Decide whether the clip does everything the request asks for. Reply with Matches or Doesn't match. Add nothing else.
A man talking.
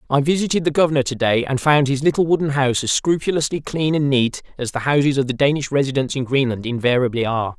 Matches